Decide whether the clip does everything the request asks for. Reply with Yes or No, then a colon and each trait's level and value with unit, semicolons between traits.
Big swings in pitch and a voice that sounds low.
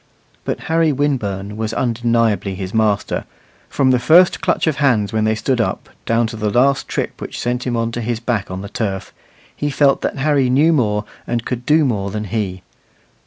No: average, 4.2 semitones; low, 115 Hz